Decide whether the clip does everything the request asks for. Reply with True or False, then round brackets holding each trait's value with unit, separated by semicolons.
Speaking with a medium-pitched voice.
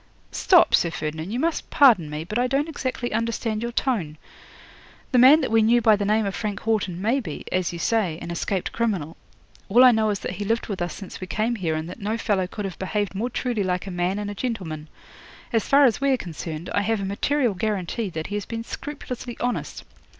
False (210 Hz)